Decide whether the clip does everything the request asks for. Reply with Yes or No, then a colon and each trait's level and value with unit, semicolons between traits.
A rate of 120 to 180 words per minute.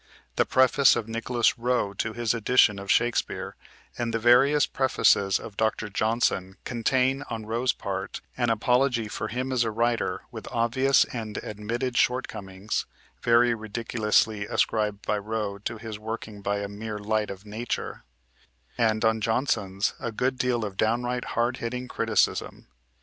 Yes: average, 150 wpm